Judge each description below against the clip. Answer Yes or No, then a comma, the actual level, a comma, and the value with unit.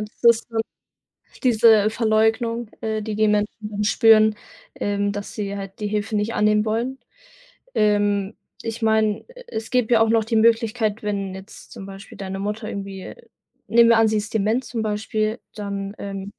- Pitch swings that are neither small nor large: No, narrow, 1.6 semitones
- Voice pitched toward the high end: Yes, high, 215 Hz